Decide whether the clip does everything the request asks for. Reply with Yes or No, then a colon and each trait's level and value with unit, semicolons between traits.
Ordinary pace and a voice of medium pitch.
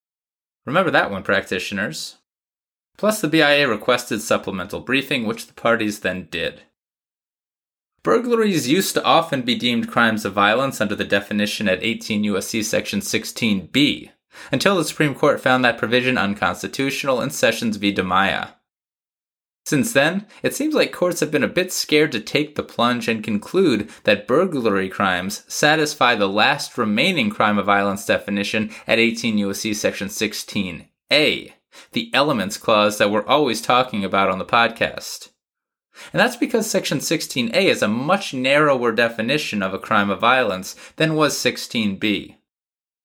No: average, 150 wpm; low, 130 Hz